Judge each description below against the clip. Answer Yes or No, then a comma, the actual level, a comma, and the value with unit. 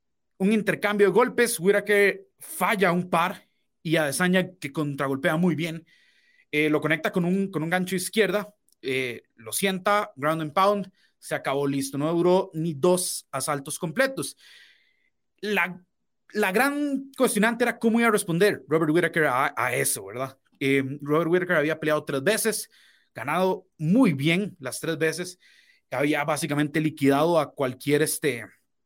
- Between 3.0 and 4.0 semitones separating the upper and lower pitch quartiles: No, average, 5.3 semitones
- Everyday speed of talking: Yes, average, 150 wpm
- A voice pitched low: No, medium, 175 Hz